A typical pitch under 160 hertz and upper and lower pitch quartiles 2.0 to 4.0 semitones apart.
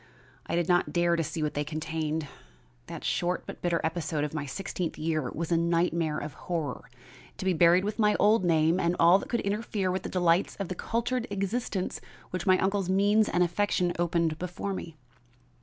No: medium, 175 Hz; average, 3.0 semitones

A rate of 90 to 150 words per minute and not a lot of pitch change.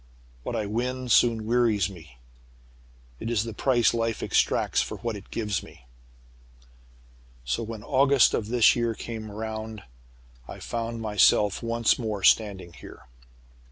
Yes: average, 140 wpm; narrow, 2.0 semitones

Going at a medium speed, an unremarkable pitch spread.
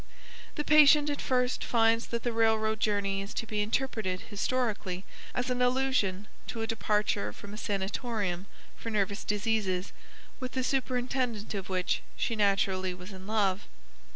Yes: average, 155 wpm; average, 3.9 semitones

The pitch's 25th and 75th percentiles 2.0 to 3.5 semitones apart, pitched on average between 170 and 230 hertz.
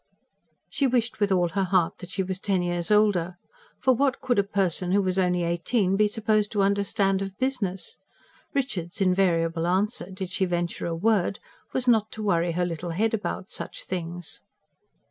Yes: average, 3.1 semitones; high, 190 Hz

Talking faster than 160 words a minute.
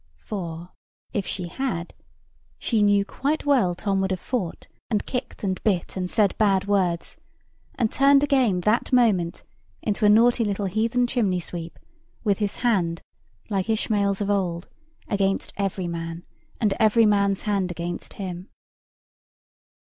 No: average, 145 wpm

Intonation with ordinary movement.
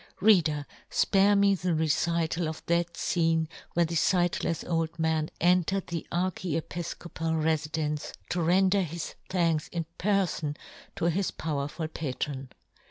No: narrow, 2.0 semitones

